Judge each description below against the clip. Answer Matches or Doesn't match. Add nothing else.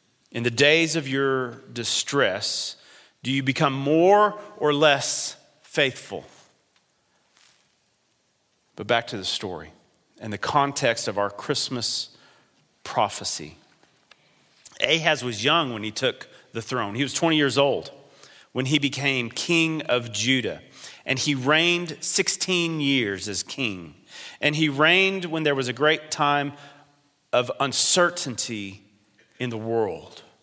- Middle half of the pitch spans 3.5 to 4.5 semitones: Matches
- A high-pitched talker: Doesn't match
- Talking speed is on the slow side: Matches